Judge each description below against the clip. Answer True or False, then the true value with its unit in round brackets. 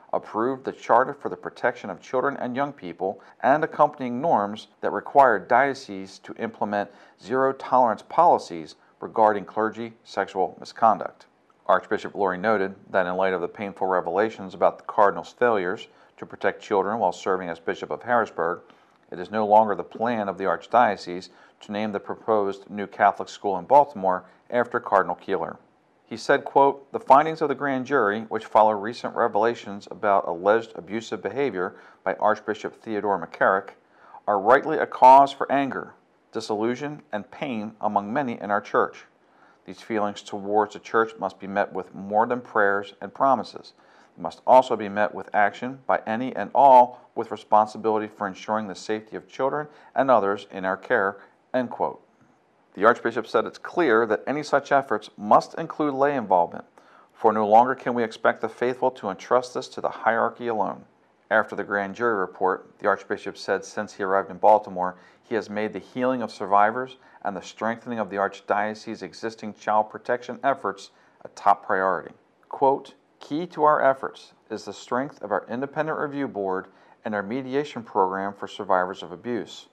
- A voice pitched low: True (110 Hz)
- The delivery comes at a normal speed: True (170 wpm)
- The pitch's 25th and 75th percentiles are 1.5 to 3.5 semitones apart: False (3.9 semitones)